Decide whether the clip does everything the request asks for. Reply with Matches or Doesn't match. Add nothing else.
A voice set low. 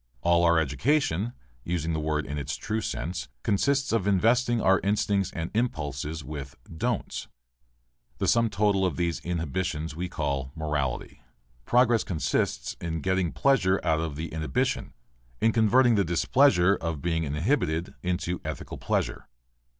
Matches